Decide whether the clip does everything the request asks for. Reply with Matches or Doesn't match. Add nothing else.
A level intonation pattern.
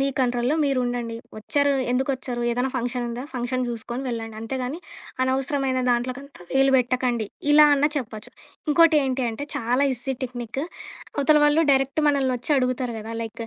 Matches